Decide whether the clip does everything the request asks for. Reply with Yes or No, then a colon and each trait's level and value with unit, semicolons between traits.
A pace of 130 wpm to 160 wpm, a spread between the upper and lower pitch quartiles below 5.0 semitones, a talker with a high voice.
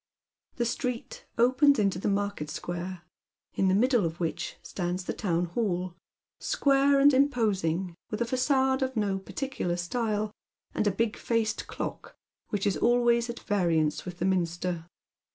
No: average, 150 wpm; wide, 5.4 semitones; high, 205 Hz